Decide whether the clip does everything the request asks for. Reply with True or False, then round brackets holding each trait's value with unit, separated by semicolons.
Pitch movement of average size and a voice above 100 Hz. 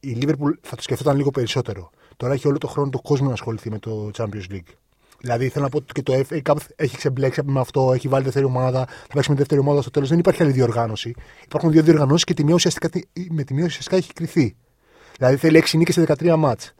True (3.5 semitones; 140 Hz)